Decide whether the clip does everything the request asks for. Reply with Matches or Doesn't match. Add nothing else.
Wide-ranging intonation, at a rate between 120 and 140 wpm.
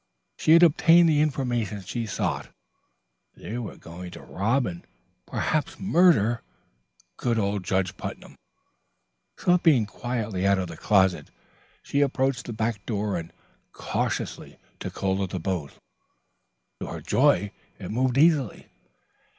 Matches